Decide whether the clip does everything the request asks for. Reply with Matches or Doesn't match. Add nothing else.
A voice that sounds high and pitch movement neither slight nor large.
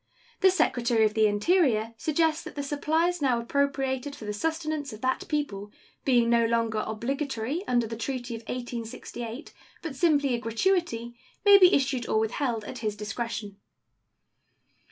Matches